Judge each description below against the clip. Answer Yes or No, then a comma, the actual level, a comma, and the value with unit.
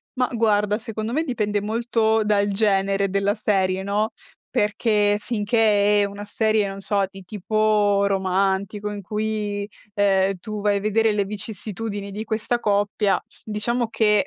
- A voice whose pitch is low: No, high, 210 Hz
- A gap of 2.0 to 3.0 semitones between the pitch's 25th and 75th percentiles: No, narrow, 1.5 semitones